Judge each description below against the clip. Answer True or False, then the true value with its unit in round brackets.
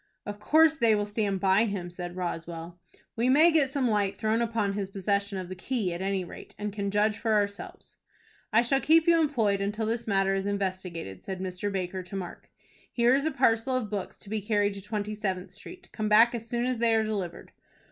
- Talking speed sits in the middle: False (220 wpm)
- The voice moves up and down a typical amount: True (3.2 semitones)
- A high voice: True (205 Hz)